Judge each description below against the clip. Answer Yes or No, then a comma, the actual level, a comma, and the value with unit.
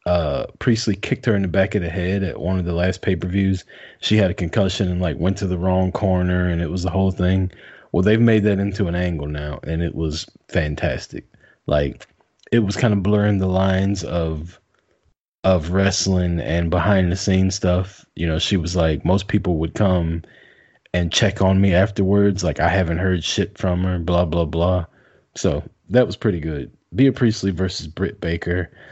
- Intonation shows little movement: Yes, narrow, 2.3 semitones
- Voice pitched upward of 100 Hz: No, very low, 90 Hz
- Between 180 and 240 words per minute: Yes, average, 200 wpm